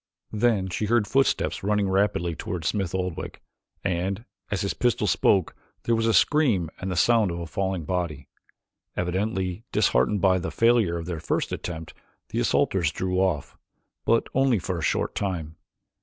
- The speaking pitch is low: Yes, very low, 95 Hz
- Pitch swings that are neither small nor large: Yes, average, 3.5 semitones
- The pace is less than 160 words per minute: No, average, 165 wpm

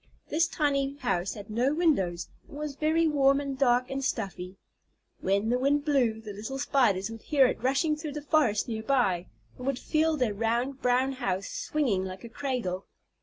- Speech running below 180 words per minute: No, average, 185 wpm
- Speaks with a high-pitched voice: Yes, very high, 255 Hz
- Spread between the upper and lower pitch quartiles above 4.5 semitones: Yes, average, 4.9 semitones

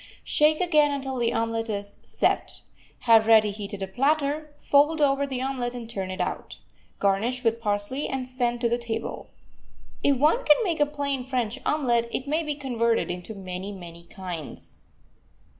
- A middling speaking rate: Yes, average, 170 wpm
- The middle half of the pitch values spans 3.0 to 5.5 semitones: Yes, average, 5.0 semitones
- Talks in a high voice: Yes, high, 240 Hz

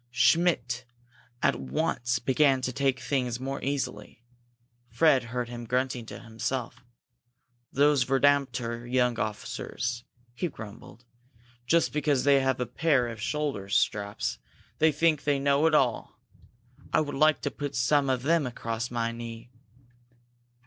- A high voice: No, low, 125 Hz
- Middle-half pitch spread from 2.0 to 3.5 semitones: Yes, average, 3.2 semitones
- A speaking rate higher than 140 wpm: No, slow, 135 wpm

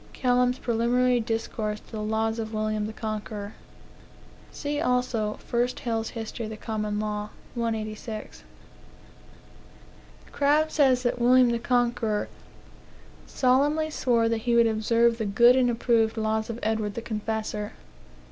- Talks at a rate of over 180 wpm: No, slow, 135 wpm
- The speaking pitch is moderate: No, high, 230 Hz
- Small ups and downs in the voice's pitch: Yes, narrow, 2.2 semitones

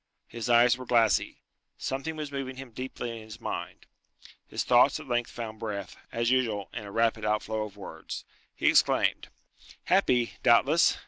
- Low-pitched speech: Yes, low, 120 Hz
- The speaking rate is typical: Yes, average, 165 wpm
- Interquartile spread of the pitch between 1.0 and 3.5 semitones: Yes, average, 2.8 semitones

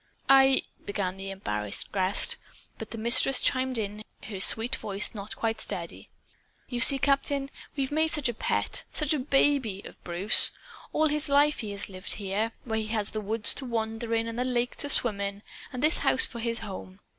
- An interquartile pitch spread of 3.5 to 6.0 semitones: Yes, average, 4.8 semitones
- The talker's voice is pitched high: Yes, high, 230 Hz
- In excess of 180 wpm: Yes, average, 200 wpm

